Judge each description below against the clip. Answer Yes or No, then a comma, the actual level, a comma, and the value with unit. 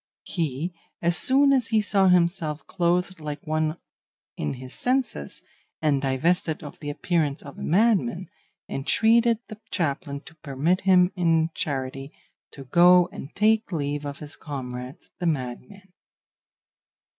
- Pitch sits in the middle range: Yes, medium, 160 Hz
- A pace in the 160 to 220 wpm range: No, slow, 135 wpm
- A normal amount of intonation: Yes, average, 4.8 semitones